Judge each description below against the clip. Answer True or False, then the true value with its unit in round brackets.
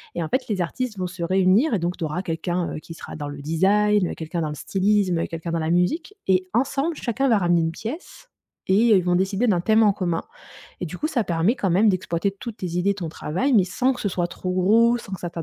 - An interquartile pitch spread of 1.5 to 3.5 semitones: False (4.0 semitones)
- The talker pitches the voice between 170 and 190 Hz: True (185 Hz)